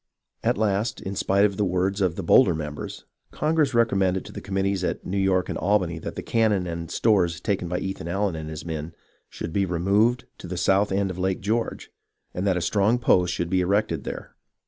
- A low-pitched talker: Yes, very low, 95 Hz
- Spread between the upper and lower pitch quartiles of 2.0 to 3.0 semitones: Yes, narrow, 2.5 semitones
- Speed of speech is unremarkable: No, fast, 215 wpm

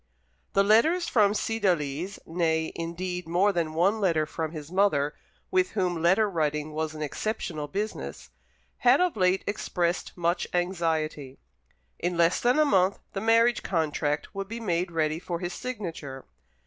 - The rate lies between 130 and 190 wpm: Yes, average, 150 wpm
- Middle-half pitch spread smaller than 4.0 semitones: No, average, 4.3 semitones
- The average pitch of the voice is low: No, medium, 175 Hz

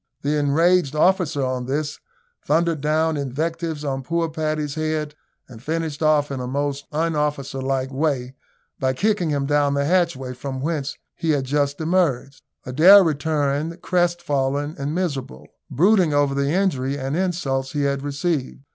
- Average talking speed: Yes, average, 155 wpm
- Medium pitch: Yes, medium, 145 Hz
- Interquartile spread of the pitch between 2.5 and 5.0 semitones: Yes, average, 2.9 semitones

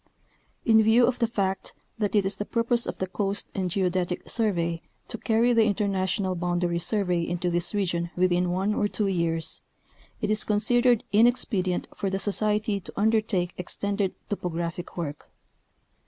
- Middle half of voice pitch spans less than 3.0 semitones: No, average, 3.3 semitones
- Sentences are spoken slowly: No, average, 155 wpm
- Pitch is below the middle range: No, high, 195 Hz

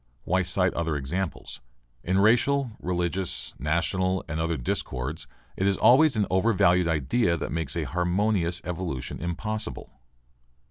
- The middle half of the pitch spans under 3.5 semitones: Yes, average, 2.9 semitones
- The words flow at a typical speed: No, slow, 130 wpm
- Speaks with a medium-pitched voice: No, very low, 90 Hz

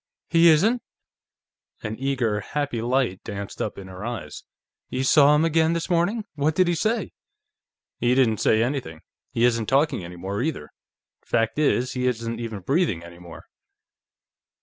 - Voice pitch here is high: No, low, 125 Hz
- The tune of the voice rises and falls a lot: Yes, wide, 6.5 semitones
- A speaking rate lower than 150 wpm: No, average, 160 wpm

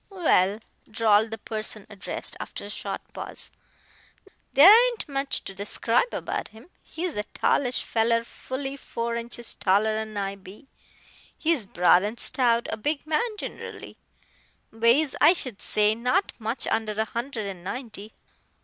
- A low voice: No, high, 230 Hz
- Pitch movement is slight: No, average, 4.4 semitones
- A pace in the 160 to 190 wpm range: No, average, 145 wpm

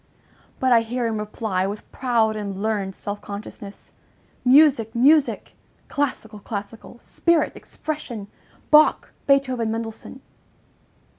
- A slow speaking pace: Yes, slow, 105 wpm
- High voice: Yes, high, 225 Hz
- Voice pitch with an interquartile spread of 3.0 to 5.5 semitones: Yes, average, 3.9 semitones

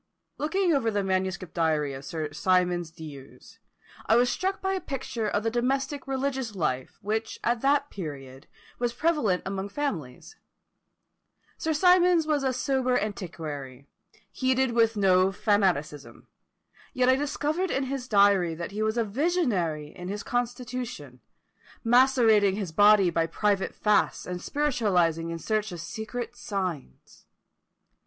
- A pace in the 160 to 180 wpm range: No, average, 140 wpm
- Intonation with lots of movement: Yes, wide, 6.9 semitones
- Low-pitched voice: No, high, 210 Hz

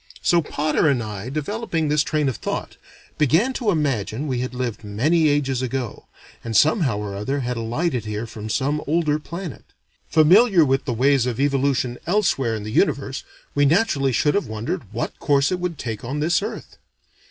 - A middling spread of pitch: Yes, average, 4.6 semitones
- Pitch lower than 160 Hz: Yes, medium, 140 Hz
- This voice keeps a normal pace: Yes, average, 180 wpm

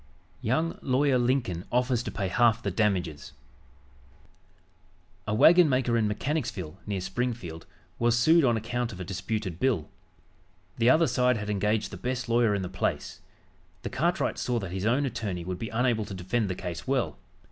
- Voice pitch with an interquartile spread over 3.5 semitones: Yes, average, 4.8 semitones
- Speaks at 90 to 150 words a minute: No, average, 170 wpm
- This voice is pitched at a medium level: No, low, 115 Hz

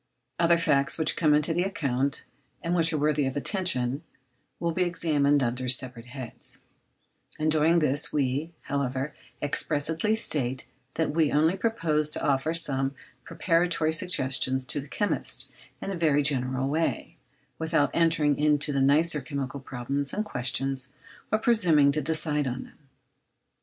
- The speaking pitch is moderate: Yes, medium, 150 Hz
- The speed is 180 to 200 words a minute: No, average, 145 wpm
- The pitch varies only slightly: No, average, 3.3 semitones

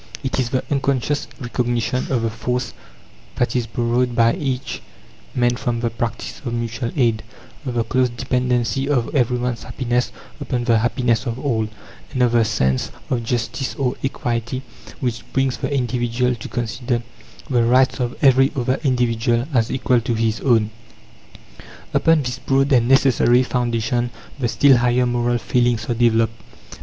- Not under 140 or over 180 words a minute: Yes, average, 160 wpm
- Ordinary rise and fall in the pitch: No, narrow, 1.6 semitones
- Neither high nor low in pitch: No, low, 120 Hz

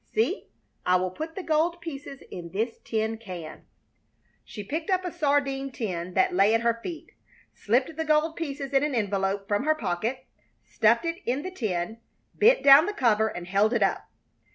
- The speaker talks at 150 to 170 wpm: No, average, 185 wpm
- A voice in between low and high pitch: No, very high, 255 Hz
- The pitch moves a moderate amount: No, wide, 7.4 semitones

